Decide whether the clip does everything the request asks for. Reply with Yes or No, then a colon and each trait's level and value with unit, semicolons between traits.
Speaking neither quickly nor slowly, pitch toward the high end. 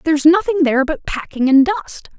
Yes: average, 190 wpm; very high, 310 Hz